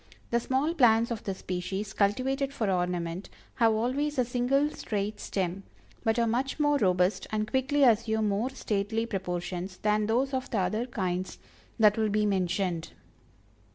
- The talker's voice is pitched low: No, high, 215 Hz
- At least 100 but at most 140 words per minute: No, average, 155 wpm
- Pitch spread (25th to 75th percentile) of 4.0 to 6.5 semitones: Yes, average, 4.5 semitones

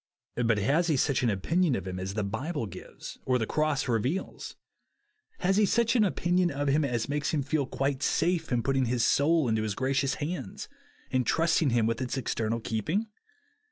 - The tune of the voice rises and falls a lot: Yes, wide, 5.8 semitones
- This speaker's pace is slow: No, average, 195 wpm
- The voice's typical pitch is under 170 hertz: Yes, low, 135 Hz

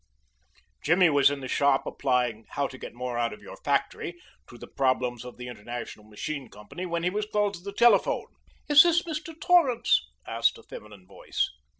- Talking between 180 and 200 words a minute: Yes, average, 190 wpm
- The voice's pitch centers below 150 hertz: Yes, medium, 140 Hz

